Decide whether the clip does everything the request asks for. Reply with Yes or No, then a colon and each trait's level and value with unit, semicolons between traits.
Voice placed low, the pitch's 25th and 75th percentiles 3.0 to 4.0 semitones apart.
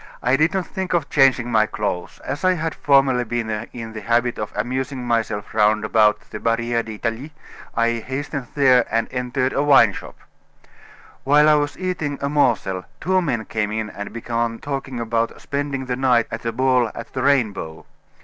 Yes: low, 125 Hz; average, 3.6 semitones